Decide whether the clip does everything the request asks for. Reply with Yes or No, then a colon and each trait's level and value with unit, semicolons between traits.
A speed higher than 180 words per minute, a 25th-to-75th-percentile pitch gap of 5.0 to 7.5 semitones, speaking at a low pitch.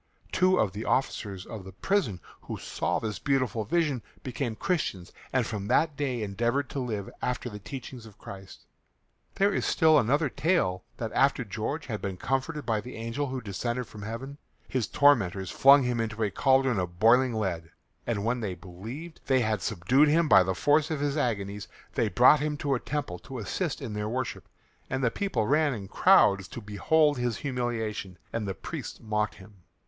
Yes: average, 190 wpm; average, 5.3 semitones; low, 120 Hz